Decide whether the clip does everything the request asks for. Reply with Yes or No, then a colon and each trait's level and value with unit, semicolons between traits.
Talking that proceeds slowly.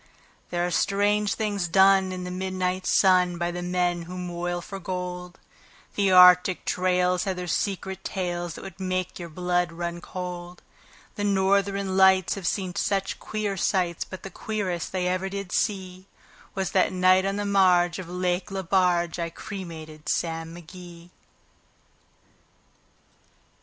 No: average, 145 wpm